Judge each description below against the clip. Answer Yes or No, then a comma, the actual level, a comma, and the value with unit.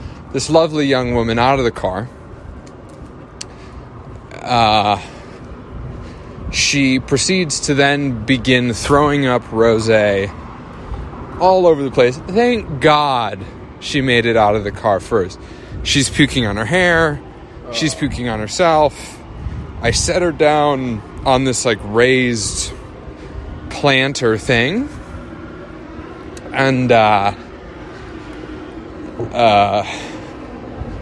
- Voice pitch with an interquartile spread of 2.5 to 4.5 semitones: No, average, 4.9 semitones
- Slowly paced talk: Yes, slow, 105 wpm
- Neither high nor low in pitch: No, low, 125 Hz